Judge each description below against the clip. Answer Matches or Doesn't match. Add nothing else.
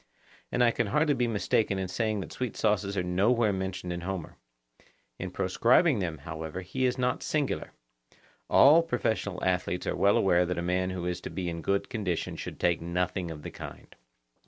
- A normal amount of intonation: Matches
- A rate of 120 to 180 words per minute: Doesn't match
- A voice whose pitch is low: Matches